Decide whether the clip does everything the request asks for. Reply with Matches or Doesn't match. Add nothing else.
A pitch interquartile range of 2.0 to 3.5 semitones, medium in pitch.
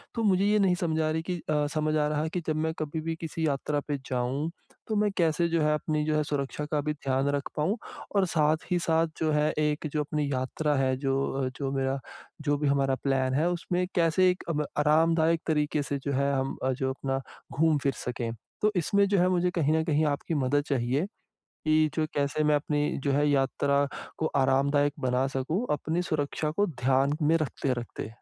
Matches